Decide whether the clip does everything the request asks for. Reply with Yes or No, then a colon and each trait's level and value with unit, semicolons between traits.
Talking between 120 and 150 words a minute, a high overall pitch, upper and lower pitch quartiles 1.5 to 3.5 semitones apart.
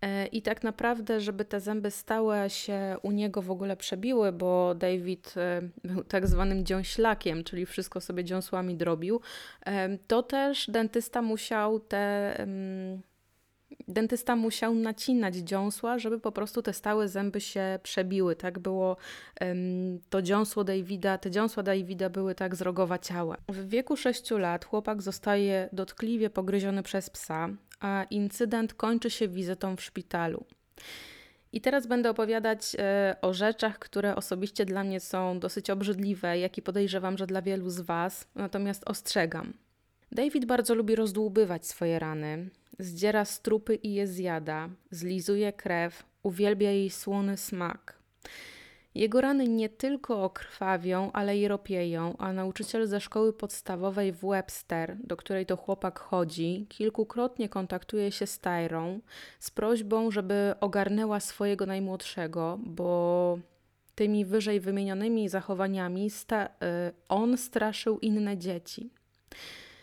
Yes: average, 130 wpm; high, 200 Hz; average, 2.7 semitones